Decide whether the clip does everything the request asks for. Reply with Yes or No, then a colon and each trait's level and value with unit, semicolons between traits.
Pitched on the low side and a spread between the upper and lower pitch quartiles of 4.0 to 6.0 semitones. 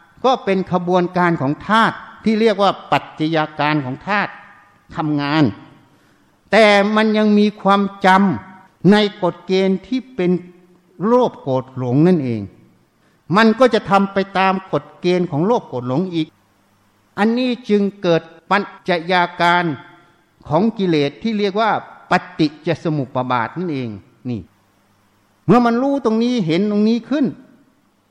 No: medium, 180 Hz; average, 5.2 semitones